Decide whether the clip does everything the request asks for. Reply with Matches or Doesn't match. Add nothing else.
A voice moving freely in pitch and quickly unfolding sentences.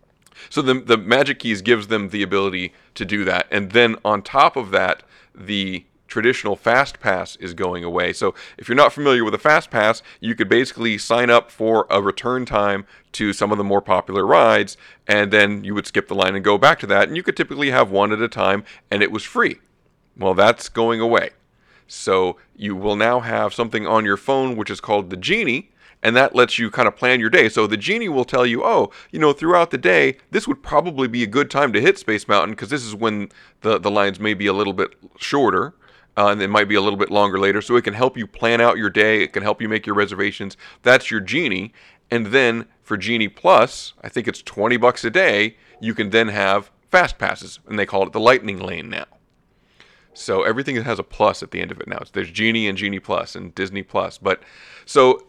Doesn't match